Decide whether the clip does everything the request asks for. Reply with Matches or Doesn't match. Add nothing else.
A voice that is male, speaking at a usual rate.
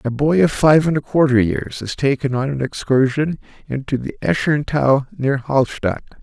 Matches